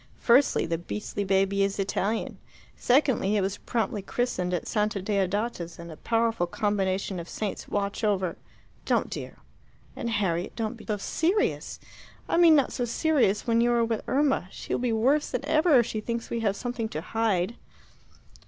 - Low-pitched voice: No, high, 215 Hz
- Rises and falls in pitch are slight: No, average, 3.6 semitones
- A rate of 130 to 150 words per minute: No, average, 180 wpm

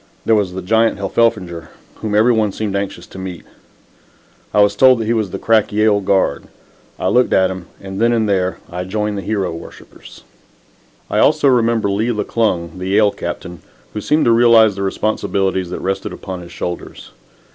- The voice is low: Yes, low, 100 Hz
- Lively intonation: No, average, 3.0 semitones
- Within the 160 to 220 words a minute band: Yes, average, 185 wpm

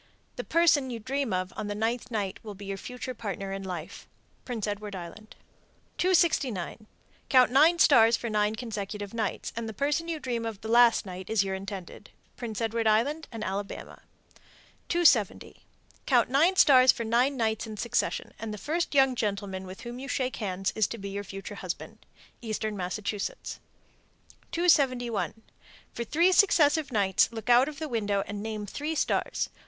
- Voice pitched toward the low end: No, high, 225 Hz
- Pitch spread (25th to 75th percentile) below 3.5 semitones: No, average, 4.3 semitones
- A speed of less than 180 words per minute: Yes, average, 170 wpm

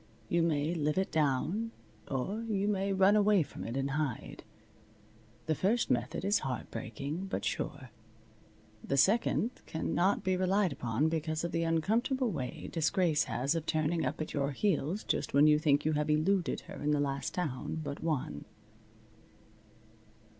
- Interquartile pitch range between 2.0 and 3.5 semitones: No, average, 4.9 semitones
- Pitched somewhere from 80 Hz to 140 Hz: No, medium, 160 Hz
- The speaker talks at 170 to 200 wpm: No, average, 160 wpm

